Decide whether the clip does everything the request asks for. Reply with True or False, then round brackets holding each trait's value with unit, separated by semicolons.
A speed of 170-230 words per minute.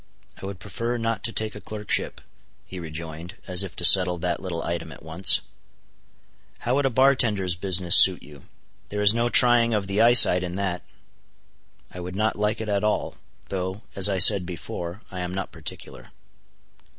True (185 wpm)